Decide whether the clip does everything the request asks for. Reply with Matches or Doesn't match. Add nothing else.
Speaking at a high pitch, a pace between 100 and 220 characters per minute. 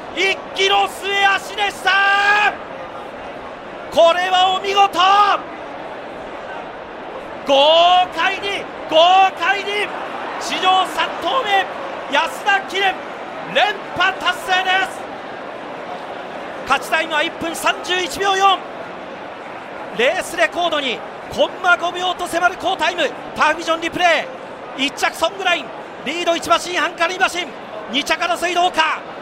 Matches